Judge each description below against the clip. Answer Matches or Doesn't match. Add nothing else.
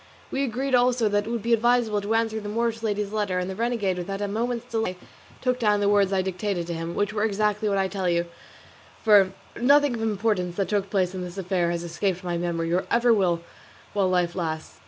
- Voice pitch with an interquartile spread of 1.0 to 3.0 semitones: Doesn't match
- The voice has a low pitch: Doesn't match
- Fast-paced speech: Matches